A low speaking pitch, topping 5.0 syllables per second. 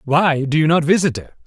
No: medium, 155 Hz; 5.4 syllables/s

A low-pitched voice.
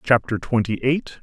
Yes: low, 120 Hz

